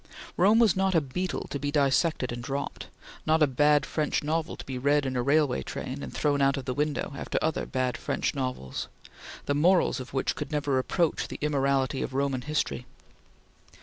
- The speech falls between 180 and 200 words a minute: Yes, average, 195 wpm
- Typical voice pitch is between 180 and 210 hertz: No, medium, 140 Hz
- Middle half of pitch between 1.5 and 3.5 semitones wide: Yes, average, 2.7 semitones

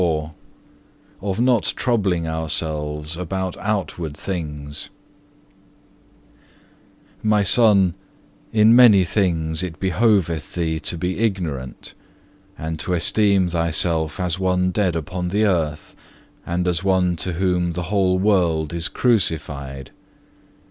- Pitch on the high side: No, very low, 90 Hz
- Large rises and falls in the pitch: No, average, 3.3 semitones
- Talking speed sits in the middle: No, slow, 115 wpm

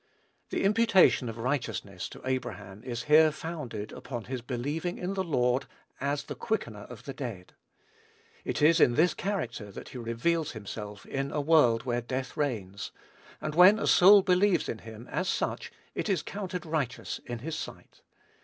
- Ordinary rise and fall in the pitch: No, wide, 6.4 semitones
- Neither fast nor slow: Yes, average, 170 wpm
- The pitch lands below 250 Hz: Yes, low, 135 Hz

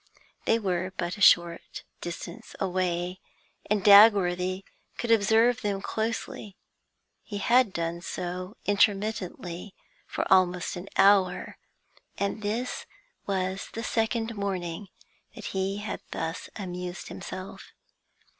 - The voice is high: Yes, high, 195 Hz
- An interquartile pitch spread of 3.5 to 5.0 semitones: No, average, 2.7 semitones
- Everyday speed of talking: No, slow, 110 wpm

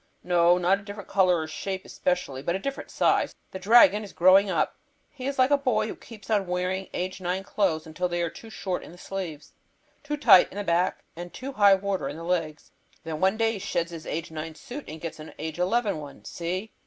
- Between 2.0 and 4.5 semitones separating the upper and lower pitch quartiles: Yes, average, 3.4 semitones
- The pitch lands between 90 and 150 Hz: No, medium, 185 Hz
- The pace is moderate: No, fast, 235 wpm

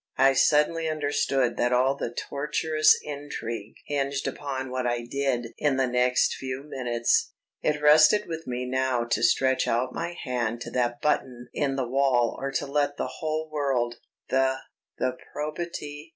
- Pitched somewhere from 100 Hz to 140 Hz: Yes, low, 135 Hz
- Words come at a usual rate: Yes, average, 160 wpm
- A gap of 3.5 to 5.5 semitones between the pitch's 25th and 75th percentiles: No, average, 3.0 semitones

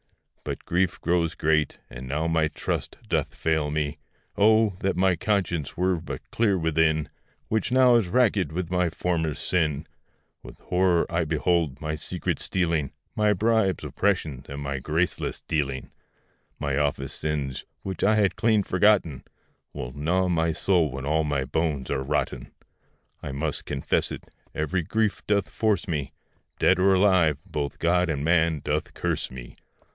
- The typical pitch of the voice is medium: No, very low, 80 Hz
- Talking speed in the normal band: Yes, average, 155 wpm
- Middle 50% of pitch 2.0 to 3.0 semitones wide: No, average, 4.0 semitones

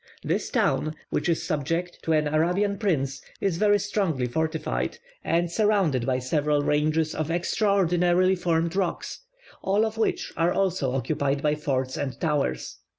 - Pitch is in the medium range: Yes, medium, 165 Hz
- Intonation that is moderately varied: Yes, average, 3.9 semitones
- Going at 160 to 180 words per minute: No, average, 150 wpm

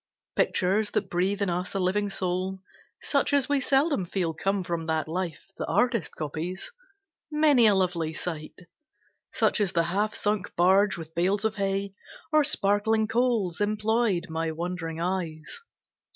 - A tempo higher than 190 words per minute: No, average, 150 wpm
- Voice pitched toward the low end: No, high, 190 Hz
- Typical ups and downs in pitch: Yes, average, 3.7 semitones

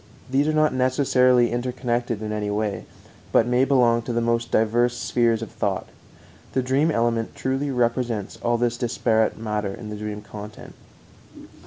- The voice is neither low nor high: No, low, 120 Hz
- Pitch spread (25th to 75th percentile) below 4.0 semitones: Yes, narrow, 2.6 semitones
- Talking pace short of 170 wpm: Yes, average, 160 wpm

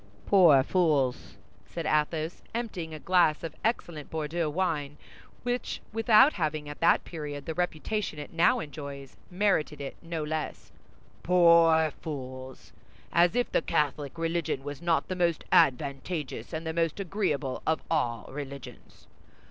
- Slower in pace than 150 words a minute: Yes, average, 140 wpm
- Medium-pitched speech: Yes, medium, 160 Hz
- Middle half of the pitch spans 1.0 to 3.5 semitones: Yes, average, 3.0 semitones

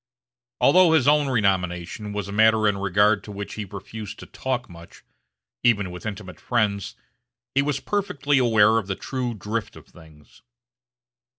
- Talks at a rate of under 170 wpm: Yes, average, 160 wpm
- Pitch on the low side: Yes, low, 105 Hz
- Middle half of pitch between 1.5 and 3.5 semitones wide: No, average, 4.0 semitones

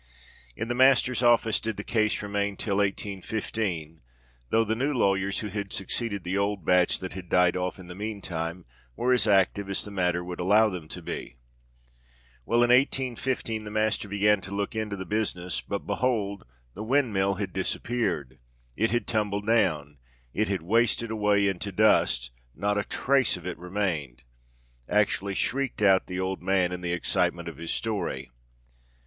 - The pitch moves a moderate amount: Yes, average, 3.6 semitones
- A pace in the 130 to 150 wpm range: No, average, 160 wpm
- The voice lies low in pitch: Yes, low, 100 Hz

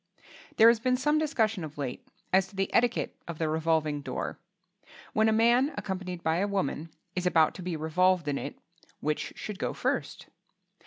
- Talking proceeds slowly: No, average, 180 wpm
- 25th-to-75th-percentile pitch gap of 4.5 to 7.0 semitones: Yes, wide, 5.6 semitones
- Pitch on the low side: No, medium, 185 Hz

